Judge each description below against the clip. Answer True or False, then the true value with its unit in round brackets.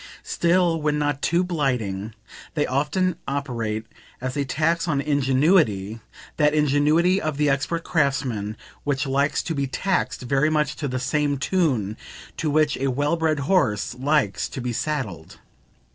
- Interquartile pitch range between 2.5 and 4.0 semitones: True (3.4 semitones)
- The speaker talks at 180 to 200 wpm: False (150 wpm)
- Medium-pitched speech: True (145 Hz)